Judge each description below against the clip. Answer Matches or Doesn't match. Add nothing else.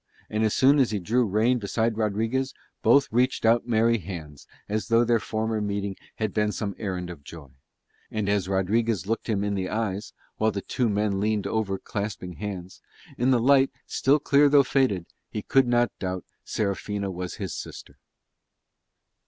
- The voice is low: Matches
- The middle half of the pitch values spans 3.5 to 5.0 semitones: Doesn't match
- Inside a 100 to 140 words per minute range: Doesn't match